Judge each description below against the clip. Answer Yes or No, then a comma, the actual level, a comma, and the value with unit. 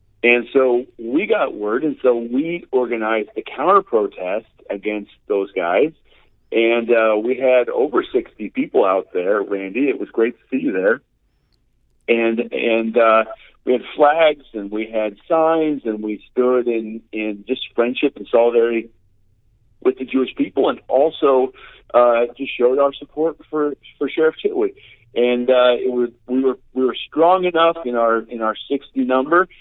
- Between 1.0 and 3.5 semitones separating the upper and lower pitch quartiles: No, average, 4.3 semitones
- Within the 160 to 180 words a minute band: Yes, average, 165 wpm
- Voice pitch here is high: No, low, 125 Hz